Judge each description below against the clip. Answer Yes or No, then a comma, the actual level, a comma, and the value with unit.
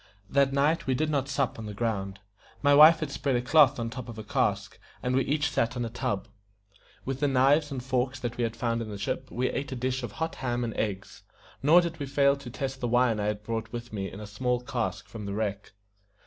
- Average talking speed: No, fast, 260 wpm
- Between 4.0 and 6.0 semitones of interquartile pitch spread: No, average, 3.6 semitones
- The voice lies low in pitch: Yes, low, 125 Hz